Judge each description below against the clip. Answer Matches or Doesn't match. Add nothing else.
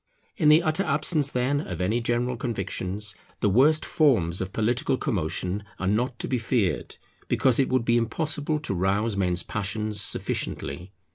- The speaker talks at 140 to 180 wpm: Matches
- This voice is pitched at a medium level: Doesn't match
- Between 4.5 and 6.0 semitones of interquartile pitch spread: Matches